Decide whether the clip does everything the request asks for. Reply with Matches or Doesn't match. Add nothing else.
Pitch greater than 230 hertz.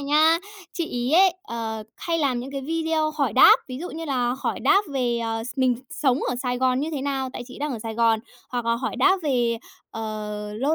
Matches